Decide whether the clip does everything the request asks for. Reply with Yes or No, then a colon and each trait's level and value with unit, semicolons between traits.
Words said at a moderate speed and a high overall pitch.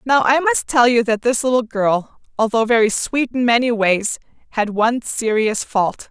Yes: average, 185 wpm; high, 235 Hz